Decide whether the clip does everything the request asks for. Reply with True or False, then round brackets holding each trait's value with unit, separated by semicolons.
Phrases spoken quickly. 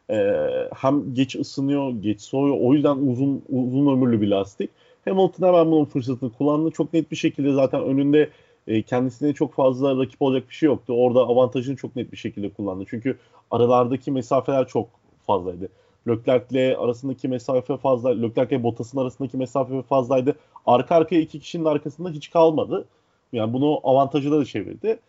True (160 wpm)